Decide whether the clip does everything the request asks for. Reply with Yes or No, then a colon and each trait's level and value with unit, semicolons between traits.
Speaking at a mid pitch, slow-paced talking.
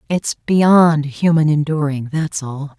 Yes: medium, 150 Hz; slow, 110 wpm